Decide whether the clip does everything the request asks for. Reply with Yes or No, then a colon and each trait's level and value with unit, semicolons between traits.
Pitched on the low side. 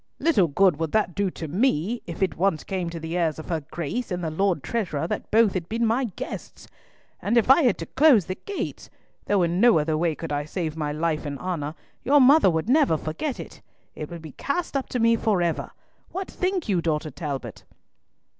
No: medium, 180 Hz